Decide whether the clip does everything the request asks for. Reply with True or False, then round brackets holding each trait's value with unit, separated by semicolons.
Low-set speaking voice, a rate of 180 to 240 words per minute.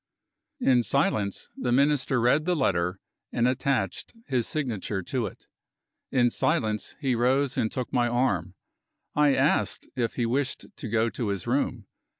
False (120 Hz; 155 wpm)